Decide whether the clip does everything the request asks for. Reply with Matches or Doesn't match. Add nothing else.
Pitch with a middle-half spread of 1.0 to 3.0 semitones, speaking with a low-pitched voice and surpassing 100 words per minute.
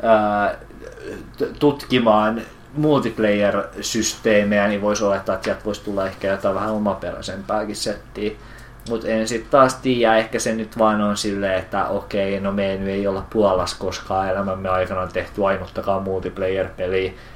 Matches